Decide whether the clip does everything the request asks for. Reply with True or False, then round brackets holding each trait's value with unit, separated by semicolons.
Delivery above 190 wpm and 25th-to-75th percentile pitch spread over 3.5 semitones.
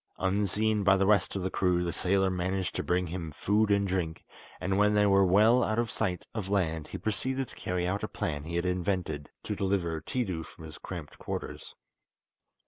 False (205 wpm; 2.6 semitones)